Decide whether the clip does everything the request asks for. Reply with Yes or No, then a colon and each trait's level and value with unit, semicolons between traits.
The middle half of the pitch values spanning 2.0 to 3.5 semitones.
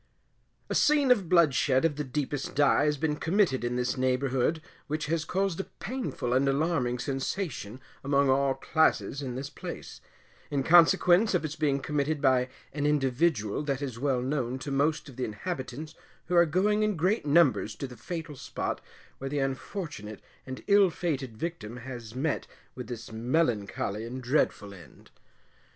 No: average, 4.2 semitones